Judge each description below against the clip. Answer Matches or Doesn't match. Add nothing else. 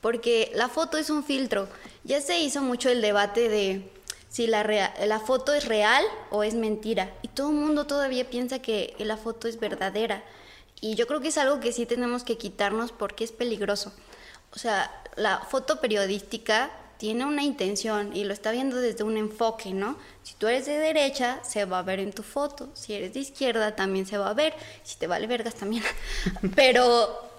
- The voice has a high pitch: Matches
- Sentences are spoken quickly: Matches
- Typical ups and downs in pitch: Matches